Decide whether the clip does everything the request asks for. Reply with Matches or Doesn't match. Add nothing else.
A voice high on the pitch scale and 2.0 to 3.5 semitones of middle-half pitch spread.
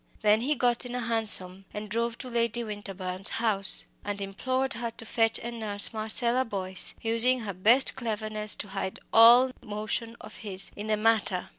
Matches